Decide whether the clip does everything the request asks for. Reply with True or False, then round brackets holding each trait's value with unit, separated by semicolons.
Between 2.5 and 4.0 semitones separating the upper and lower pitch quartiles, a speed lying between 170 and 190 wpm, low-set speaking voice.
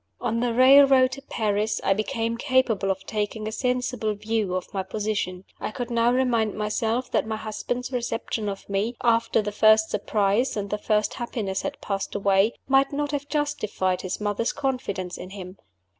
False (3.4 semitones; 175 wpm; 220 Hz)